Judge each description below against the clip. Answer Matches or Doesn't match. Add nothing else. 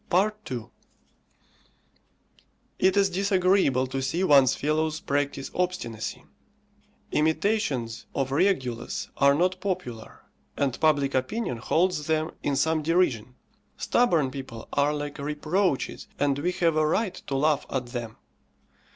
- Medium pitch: Matches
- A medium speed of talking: Doesn't match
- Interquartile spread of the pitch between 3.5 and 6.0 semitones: Matches